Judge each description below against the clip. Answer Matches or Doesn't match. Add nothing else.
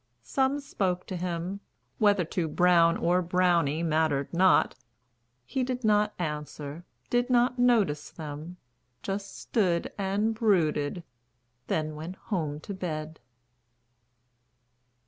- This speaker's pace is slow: Matches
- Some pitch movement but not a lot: Matches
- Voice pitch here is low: Doesn't match